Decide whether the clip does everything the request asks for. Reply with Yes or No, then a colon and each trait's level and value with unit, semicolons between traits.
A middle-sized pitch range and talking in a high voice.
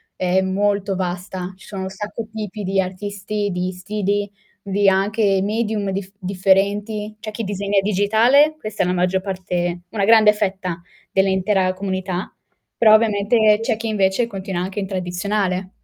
No: narrow, 1.9 semitones; high, 195 Hz